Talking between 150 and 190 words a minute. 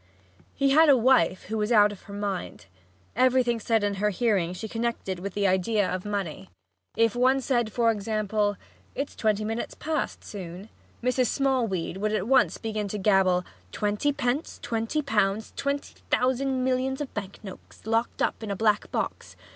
Yes: average, 170 wpm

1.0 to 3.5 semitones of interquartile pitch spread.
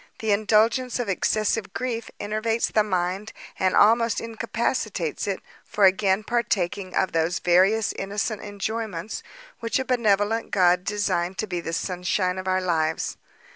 Yes: average, 3.2 semitones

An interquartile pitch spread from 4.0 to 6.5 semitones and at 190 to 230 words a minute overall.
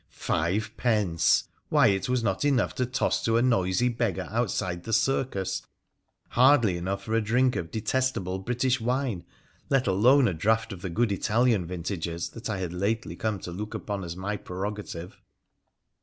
No: average, 4.6 semitones; average, 170 wpm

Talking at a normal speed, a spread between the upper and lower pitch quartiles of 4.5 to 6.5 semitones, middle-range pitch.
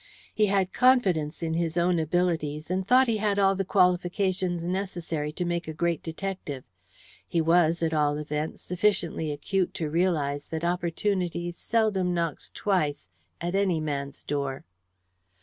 No: average, 150 wpm; average, 3.3 semitones; medium, 175 Hz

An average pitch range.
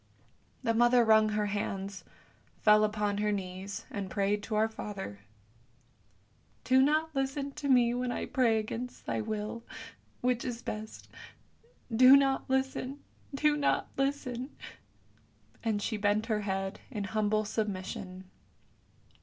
Yes: average, 3.7 semitones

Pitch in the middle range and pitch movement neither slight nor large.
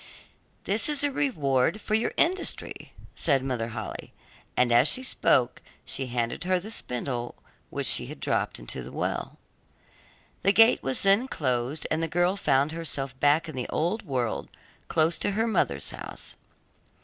No: medium, 150 Hz; wide, 7.8 semitones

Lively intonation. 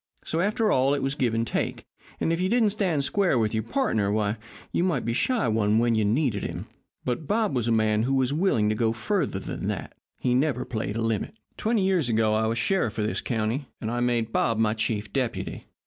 Yes: wide, 6.4 semitones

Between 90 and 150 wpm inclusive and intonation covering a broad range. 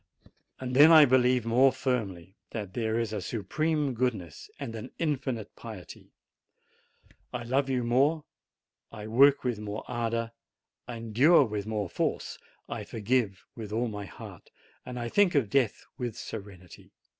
No: average, 145 wpm; average, 3.5 semitones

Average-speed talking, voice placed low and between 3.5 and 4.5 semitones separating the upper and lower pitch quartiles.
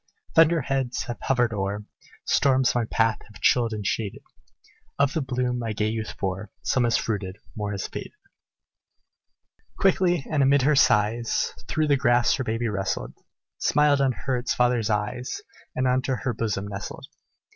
Yes: average, 160 wpm; low, 120 Hz; average, 4.0 semitones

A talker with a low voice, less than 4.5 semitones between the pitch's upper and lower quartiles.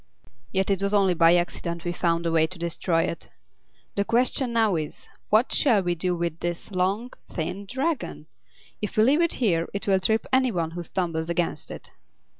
No: medium, 185 Hz; average, 4.1 semitones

